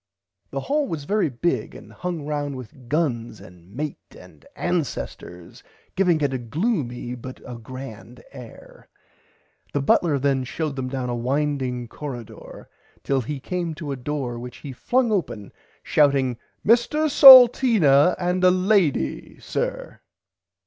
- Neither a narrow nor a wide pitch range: No, wide, 6.0 semitones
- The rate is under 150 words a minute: Yes, average, 140 wpm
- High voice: No, medium, 140 Hz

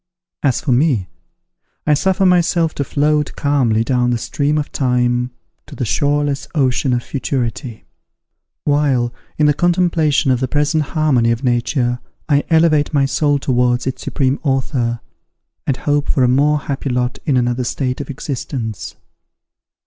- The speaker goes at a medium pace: Yes, average, 150 wpm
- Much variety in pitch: No, average, 3.2 semitones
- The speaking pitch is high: No, medium, 140 Hz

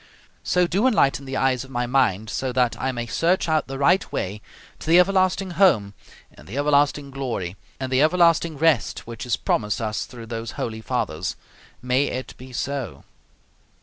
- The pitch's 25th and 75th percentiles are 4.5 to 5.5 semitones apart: Yes, average, 5.2 semitones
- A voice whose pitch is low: Yes, low, 130 Hz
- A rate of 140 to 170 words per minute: No, average, 180 wpm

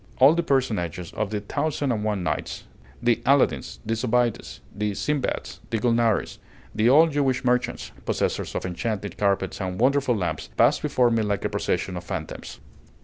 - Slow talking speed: No, average, 165 wpm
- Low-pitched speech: Yes, low, 115 Hz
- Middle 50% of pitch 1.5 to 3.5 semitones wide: No, average, 4.4 semitones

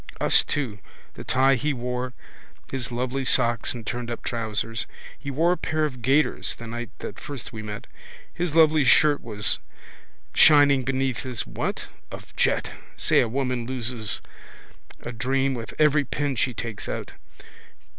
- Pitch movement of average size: Yes, average, 3.0 semitones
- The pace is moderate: Yes, average, 155 wpm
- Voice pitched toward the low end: Yes, low, 130 Hz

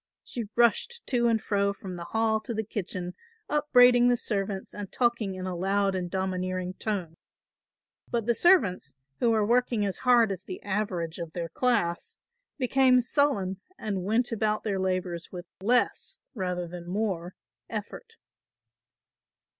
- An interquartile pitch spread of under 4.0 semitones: No, average, 4.4 semitones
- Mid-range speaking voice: No, high, 200 Hz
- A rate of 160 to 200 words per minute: No, average, 150 wpm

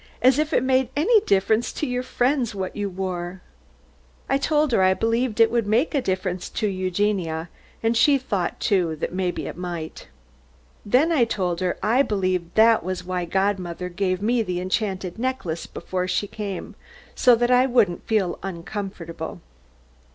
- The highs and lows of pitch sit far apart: No, average, 4.8 semitones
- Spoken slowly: No, average, 165 wpm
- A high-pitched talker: Yes, high, 200 Hz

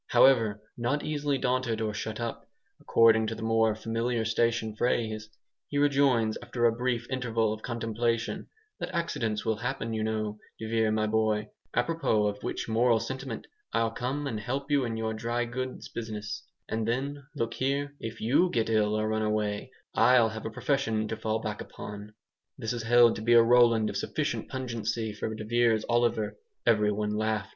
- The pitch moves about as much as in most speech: No, narrow, 2.1 semitones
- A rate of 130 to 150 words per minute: No, average, 180 wpm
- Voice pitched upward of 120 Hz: No, low, 115 Hz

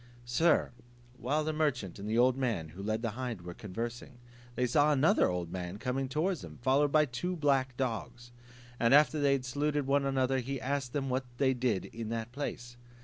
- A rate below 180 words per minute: No, average, 195 wpm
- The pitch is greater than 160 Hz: No, low, 130 Hz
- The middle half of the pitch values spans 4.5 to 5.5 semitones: No, average, 3.4 semitones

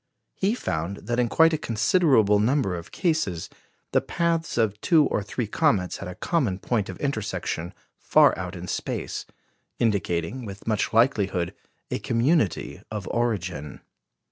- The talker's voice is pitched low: Yes, low, 110 Hz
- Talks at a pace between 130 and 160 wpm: Yes, average, 145 wpm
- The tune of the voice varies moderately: No, wide, 6.7 semitones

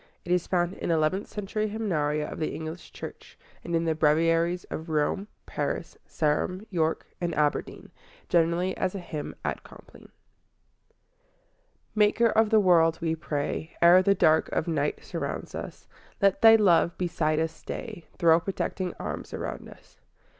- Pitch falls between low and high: Yes, medium, 170 Hz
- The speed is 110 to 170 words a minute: Yes, average, 155 wpm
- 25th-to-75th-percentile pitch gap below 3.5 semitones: Yes, average, 3.0 semitones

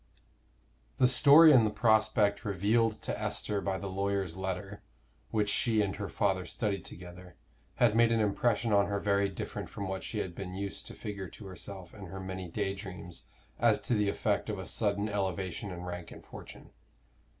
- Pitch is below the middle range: Yes, low, 100 Hz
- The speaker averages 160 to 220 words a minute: Yes, average, 185 wpm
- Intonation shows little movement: Yes, narrow, 2.1 semitones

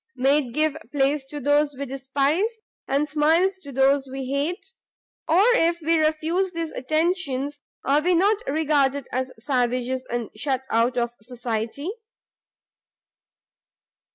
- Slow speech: Yes, slow, 125 wpm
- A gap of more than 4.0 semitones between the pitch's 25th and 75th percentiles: No, average, 3.5 semitones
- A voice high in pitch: Yes, very high, 285 Hz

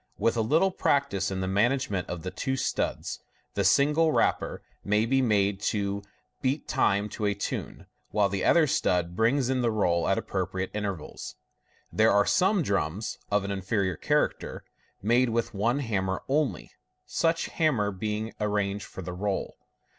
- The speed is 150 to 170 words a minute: Yes, average, 160 wpm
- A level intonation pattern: No, average, 4.7 semitones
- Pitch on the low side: Yes, low, 105 Hz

